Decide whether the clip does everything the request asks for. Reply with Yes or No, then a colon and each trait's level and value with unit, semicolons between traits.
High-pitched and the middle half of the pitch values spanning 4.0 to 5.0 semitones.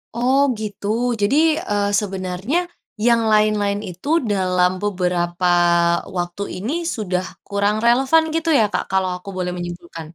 No: high, 200 Hz; average, 2.9 semitones